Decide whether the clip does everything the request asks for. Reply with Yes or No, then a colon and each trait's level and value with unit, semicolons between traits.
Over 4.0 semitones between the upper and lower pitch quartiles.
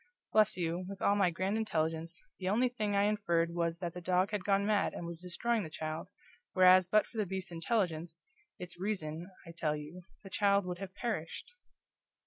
No: average, 3.3 semitones